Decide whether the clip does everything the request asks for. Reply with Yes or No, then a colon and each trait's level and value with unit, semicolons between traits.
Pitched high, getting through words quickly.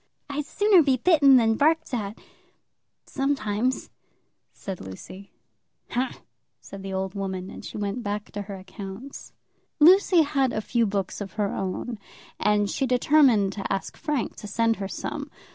No: high, 220 Hz; average, 160 wpm